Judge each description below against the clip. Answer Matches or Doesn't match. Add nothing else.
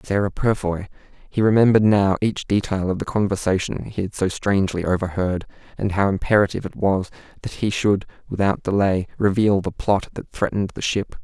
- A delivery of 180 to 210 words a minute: Doesn't match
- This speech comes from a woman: Doesn't match